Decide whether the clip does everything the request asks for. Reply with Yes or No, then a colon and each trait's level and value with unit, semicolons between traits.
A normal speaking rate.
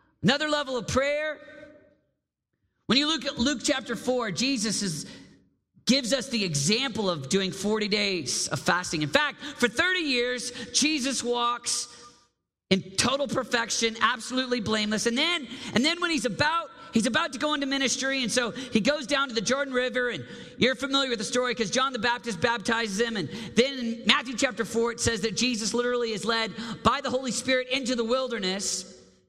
Yes: average, 180 wpm